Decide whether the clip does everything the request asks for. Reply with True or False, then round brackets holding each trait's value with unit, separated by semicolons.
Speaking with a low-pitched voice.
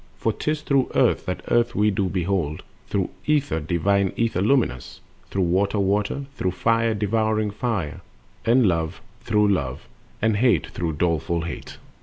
True (100 Hz)